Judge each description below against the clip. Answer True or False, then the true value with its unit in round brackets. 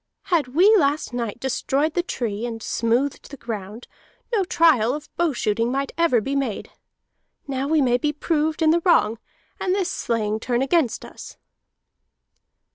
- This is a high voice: True (275 Hz)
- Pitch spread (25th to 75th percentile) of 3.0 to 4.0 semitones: False (5.4 semitones)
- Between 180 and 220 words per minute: False (160 wpm)